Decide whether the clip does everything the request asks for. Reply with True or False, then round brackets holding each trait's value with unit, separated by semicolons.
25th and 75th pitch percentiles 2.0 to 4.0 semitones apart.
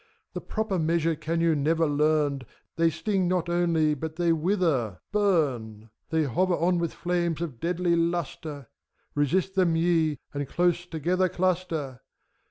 True (2.8 semitones)